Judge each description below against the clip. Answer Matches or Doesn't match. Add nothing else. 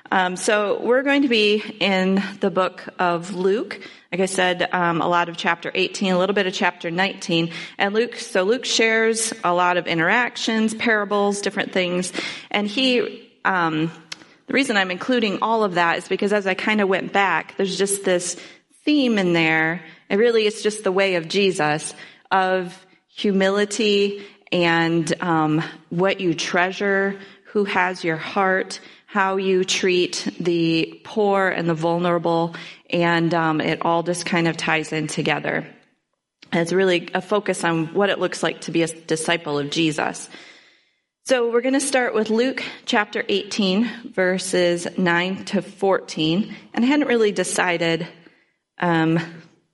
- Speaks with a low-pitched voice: Doesn't match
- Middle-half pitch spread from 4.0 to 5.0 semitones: Doesn't match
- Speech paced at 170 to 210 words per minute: Doesn't match